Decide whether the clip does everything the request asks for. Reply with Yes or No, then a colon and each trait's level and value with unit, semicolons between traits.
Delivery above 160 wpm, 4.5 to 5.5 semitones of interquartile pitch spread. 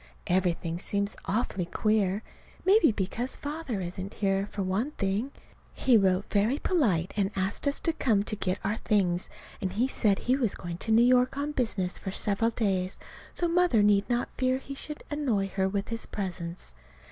Yes: average, 180 wpm; average, 4.8 semitones